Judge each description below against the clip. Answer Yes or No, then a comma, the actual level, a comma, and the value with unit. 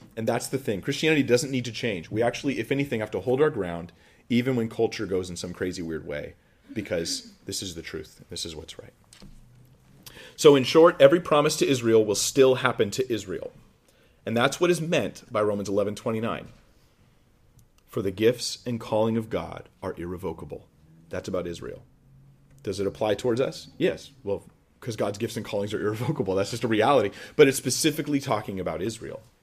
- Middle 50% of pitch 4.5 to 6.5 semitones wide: Yes, average, 4.8 semitones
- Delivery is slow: No, average, 190 wpm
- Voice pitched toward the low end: Yes, low, 120 Hz